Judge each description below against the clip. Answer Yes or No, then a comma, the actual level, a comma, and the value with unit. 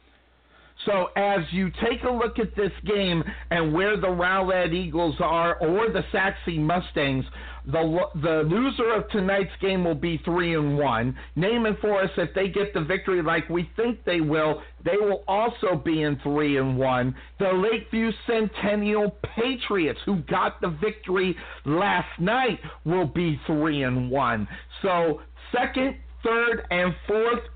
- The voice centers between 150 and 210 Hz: Yes, medium, 185 Hz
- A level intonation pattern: No, average, 4.5 semitones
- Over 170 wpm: No, average, 155 wpm